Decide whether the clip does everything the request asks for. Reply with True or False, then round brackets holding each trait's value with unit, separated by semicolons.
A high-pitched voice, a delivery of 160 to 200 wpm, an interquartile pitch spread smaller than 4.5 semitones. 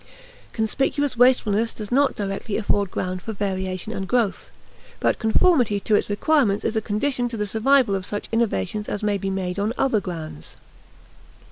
True (210 Hz; 165 wpm; 3.2 semitones)